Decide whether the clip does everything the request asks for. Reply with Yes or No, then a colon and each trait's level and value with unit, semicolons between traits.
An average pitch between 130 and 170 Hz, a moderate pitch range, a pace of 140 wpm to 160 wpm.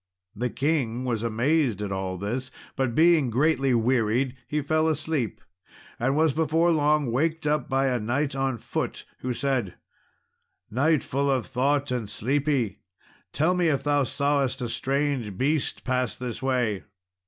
Yes: low, 135 Hz; average, 3.6 semitones; average, 155 wpm